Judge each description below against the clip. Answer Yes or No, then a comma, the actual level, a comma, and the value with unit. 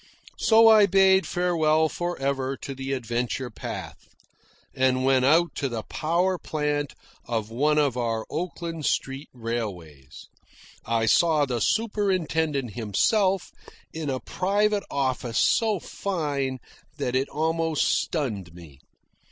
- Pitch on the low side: No, medium, 145 Hz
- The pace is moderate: No, slow, 125 wpm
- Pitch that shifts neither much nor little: No, wide, 5.8 semitones